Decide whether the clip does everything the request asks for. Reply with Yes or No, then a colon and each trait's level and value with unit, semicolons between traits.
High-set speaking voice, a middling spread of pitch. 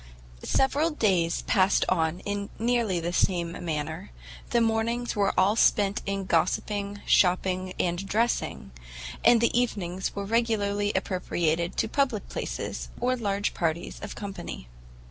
Yes: high, 200 Hz; average, 4.3 semitones